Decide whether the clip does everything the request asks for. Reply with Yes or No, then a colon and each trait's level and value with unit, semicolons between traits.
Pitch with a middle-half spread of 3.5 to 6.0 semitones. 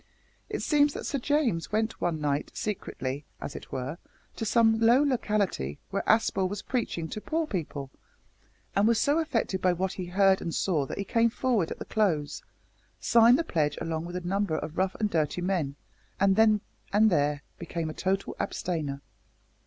Yes: wide, 5.6 semitones